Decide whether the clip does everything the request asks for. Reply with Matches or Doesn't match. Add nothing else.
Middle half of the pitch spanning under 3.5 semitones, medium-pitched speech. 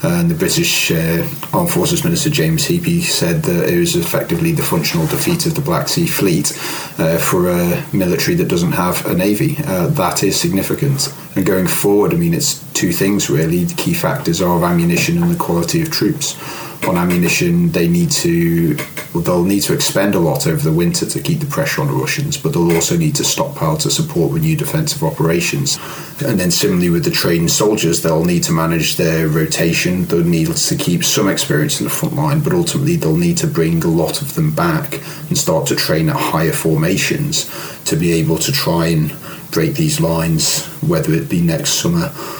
Matches